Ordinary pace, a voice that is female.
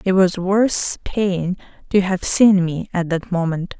Yes: average, 175 wpm; female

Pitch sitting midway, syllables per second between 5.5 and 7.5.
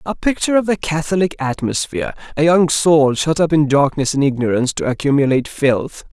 Yes: medium, 150 Hz; 5.8 syllables/s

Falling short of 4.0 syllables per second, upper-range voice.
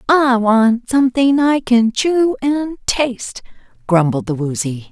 Yes: 3.8 syllables/s; high, 240 Hz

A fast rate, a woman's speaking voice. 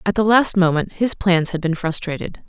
Yes: fast, 220 wpm; female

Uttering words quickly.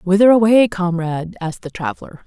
No: average, 160 wpm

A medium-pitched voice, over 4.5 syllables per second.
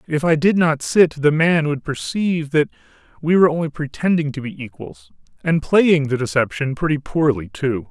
Yes: medium, 145 Hz; 5.1 syllables/s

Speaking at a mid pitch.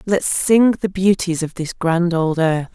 Yes: medium, 180 Hz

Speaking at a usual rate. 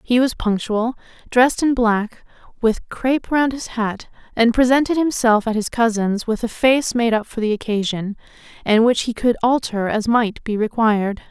Yes: average, 180 wpm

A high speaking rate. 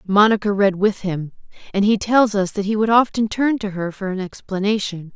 Yes: fast, 210 wpm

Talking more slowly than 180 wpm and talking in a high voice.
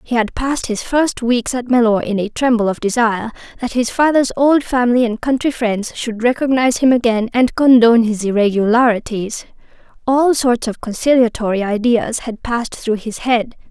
Yes: average, 170 wpm; high, 235 Hz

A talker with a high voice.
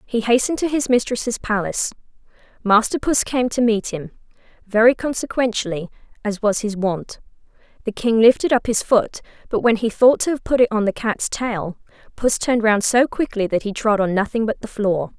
Yes: high, 220 Hz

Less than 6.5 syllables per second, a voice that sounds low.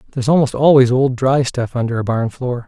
Yes: 5.9 syllables/s; low, 125 Hz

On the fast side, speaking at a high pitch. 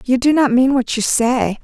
Yes: fast, 255 wpm; very high, 250 Hz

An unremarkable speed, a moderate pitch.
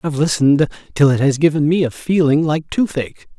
Yes: average, 195 wpm; medium, 150 Hz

